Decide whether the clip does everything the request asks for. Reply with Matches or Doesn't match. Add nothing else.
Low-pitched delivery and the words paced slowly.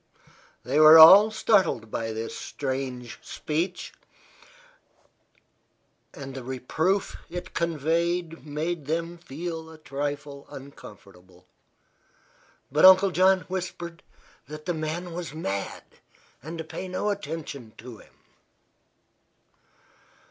Doesn't match